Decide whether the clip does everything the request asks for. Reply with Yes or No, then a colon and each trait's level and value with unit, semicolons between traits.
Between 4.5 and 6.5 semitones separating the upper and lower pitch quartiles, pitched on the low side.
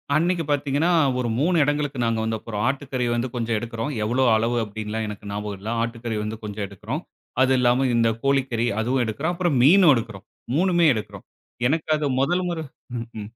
Yes: average, 4.9 semitones; low, 120 Hz